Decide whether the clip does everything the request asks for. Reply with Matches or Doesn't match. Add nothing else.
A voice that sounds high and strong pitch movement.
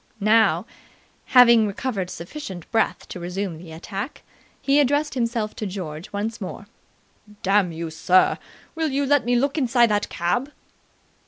Matches